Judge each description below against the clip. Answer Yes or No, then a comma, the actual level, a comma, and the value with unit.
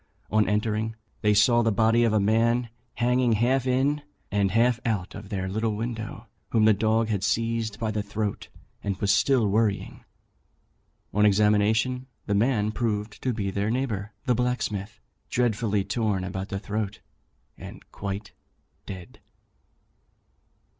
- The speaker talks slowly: No, average, 145 wpm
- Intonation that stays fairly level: Yes, narrow, 2.3 semitones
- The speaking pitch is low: Yes, low, 110 Hz